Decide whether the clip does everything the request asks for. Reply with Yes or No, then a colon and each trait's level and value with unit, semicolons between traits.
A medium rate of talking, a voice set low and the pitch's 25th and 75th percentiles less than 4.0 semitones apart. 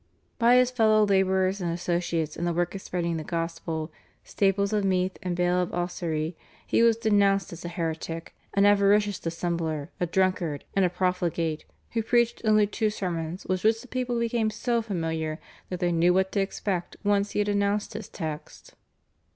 No: average, 180 wpm; medium, 185 Hz; average, 3.4 semitones